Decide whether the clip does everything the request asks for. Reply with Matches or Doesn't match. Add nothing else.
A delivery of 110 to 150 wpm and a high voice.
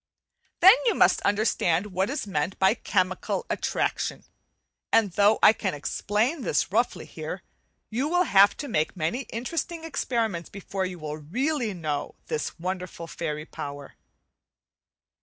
Matches